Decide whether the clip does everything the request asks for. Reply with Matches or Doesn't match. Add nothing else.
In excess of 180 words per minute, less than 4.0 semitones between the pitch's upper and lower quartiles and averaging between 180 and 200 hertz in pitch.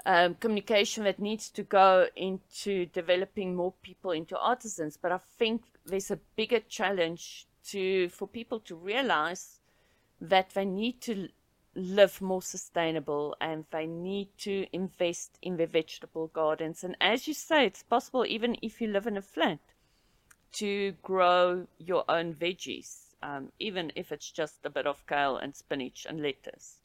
Doesn't match